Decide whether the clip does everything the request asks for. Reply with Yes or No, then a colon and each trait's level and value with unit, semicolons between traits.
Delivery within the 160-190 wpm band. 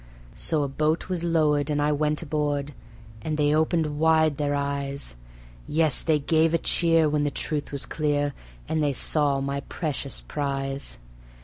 Yes: average, 165 wpm